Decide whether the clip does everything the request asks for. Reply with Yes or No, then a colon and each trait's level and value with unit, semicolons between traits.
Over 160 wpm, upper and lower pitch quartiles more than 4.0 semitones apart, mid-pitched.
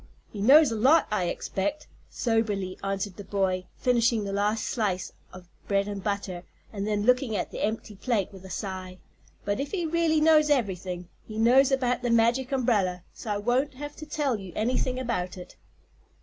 No: average, 185 wpm; average, 4.7 semitones; high, 220 Hz